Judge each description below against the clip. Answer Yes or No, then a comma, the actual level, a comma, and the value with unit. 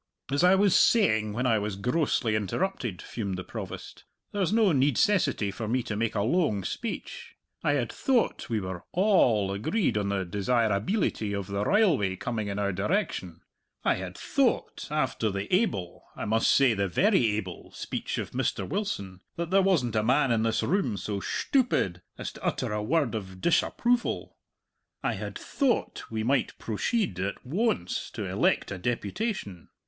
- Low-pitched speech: Yes, low, 115 Hz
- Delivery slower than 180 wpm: Yes, average, 170 wpm